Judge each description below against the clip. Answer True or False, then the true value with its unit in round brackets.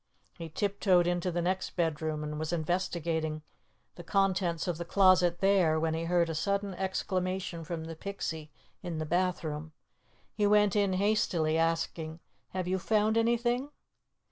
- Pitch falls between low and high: True (175 Hz)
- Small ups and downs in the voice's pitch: False (3.1 semitones)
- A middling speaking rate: True (150 wpm)